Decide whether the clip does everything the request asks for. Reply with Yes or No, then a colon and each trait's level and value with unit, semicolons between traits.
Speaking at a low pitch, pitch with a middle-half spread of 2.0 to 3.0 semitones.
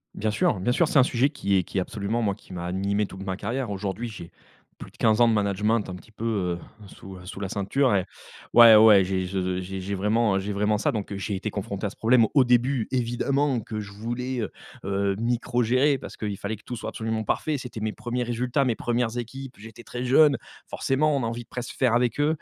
No: low, 110 Hz; average, 3.6 semitones